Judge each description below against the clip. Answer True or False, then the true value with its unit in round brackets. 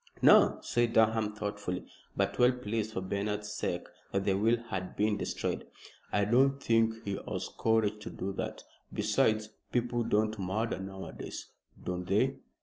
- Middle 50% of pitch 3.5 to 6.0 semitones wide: False (2.4 semitones)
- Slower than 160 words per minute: True (150 wpm)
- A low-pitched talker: True (105 Hz)